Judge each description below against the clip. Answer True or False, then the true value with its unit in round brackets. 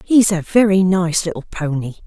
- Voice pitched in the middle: True (180 Hz)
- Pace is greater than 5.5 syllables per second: False (4.7 syllables/s)